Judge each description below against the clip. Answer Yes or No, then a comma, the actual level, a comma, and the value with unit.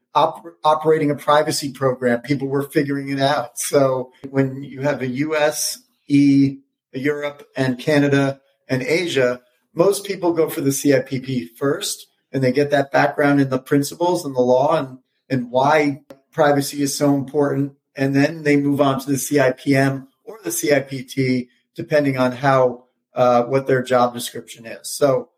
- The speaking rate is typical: Yes, average, 160 wpm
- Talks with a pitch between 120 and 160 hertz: Yes, medium, 140 Hz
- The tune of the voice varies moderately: No, narrow, 2.0 semitones